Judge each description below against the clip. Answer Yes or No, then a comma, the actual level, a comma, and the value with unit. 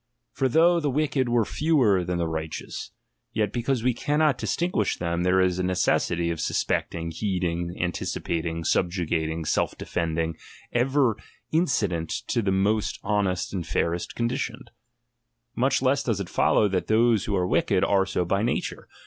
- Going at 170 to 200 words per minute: No, average, 155 wpm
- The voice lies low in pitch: Yes, very low, 95 Hz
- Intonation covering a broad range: Yes, wide, 5.9 semitones